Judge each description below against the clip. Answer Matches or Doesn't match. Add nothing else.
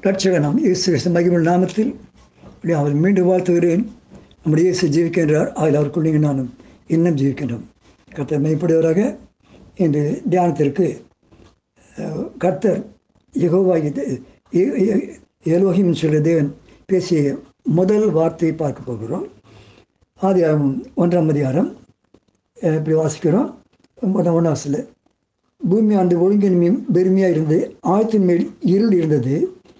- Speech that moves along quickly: Doesn't match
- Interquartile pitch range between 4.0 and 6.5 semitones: Doesn't match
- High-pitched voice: Doesn't match